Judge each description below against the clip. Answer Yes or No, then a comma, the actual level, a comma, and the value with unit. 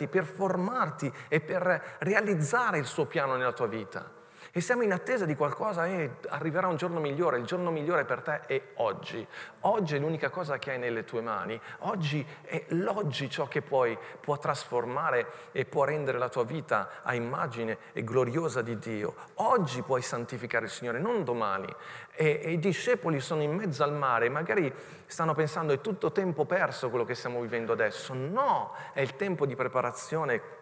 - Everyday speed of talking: No, fast, 180 wpm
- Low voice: No, medium, 155 Hz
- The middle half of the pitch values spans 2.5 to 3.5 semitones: No, wide, 5.5 semitones